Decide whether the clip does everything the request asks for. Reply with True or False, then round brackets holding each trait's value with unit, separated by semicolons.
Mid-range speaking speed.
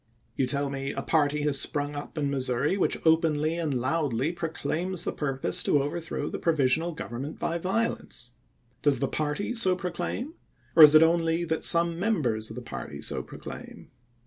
True (180 wpm)